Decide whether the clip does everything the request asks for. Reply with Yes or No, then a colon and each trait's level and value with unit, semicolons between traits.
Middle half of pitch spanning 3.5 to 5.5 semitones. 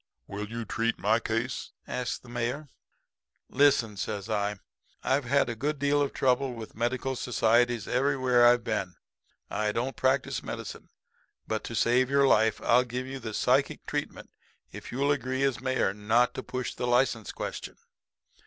No: average, 2.7 semitones